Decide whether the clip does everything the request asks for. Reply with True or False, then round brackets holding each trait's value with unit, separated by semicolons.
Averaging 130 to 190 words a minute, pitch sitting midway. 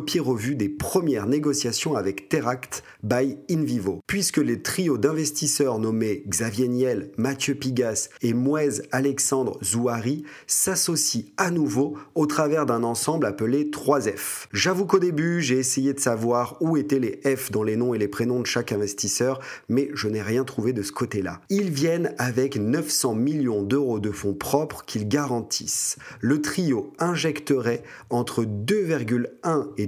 False (150 wpm; 130 Hz)